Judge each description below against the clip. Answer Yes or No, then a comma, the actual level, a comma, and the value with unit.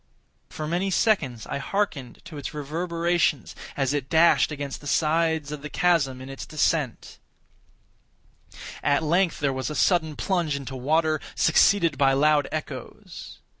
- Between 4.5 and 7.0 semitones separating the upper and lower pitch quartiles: No, average, 3.2 semitones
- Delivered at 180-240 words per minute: No, average, 145 wpm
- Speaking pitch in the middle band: Yes, medium, 150 Hz